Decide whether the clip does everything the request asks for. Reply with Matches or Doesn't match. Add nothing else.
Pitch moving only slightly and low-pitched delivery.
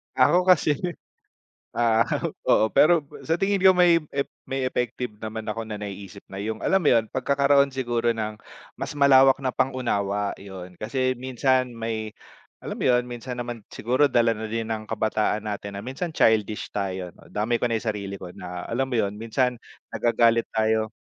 Doesn't match